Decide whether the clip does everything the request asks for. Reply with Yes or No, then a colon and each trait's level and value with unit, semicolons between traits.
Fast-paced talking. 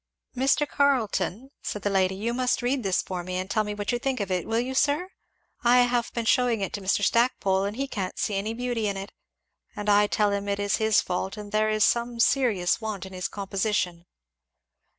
Yes: fast, 220 wpm